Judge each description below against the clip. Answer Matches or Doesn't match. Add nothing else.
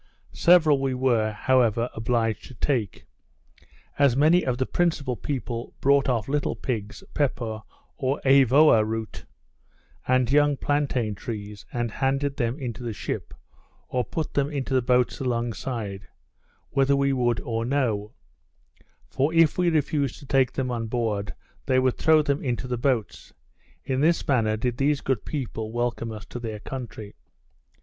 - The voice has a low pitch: Matches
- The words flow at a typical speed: Matches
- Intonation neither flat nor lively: Matches